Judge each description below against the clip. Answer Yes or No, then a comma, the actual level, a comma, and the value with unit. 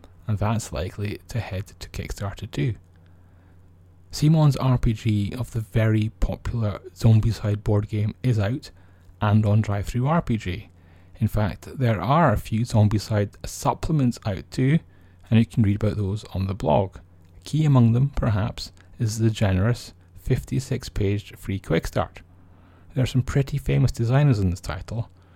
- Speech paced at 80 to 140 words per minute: No, average, 150 wpm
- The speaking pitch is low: Yes, low, 105 Hz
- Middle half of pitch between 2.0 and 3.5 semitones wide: No, average, 4.3 semitones